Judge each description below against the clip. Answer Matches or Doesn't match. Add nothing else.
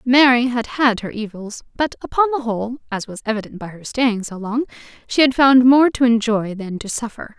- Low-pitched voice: Doesn't match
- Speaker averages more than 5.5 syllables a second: Doesn't match